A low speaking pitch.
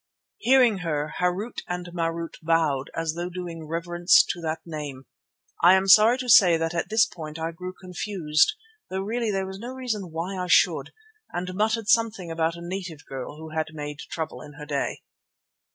No: medium, 175 Hz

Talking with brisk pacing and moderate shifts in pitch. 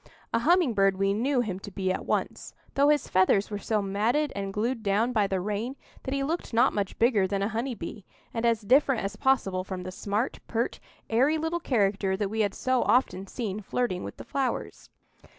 Yes: fast, 210 wpm; average, 4.5 semitones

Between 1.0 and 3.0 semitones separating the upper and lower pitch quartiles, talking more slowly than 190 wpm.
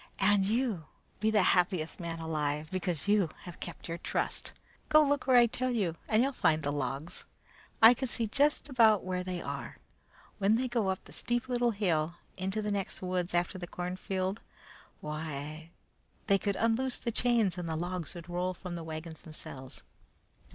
No: average, 5.2 semitones; average, 180 wpm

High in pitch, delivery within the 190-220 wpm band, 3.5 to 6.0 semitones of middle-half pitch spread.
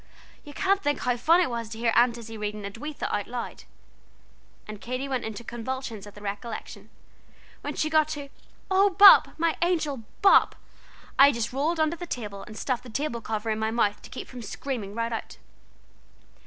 Yes: high, 240 Hz; average, 195 wpm; average, 5.3 semitones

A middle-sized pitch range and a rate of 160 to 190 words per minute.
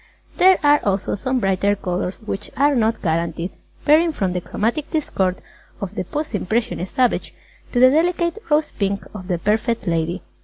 No: wide, 7.8 semitones; average, 165 wpm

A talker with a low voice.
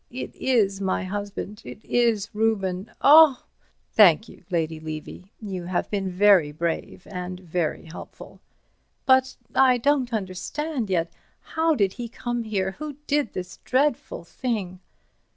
No: high, 205 Hz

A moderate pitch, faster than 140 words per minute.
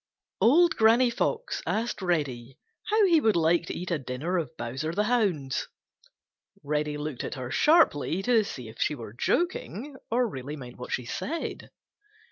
Yes: medium, 170 Hz; average, 165 wpm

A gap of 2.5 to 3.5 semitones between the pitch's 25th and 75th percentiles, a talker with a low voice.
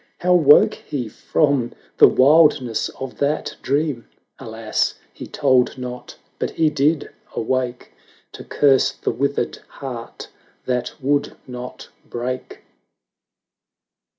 Yes: average, 2.8 semitones; low, 130 Hz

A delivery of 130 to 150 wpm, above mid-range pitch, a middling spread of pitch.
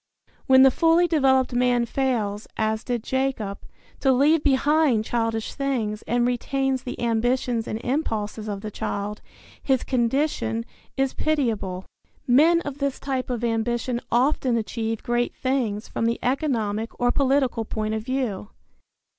Yes: average, 140 wpm; high, 245 Hz; average, 3.3 semitones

